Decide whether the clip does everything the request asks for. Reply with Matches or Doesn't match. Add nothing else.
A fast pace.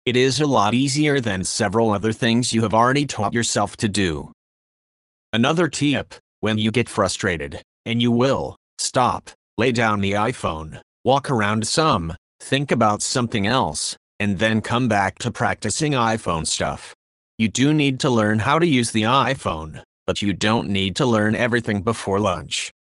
Doesn't match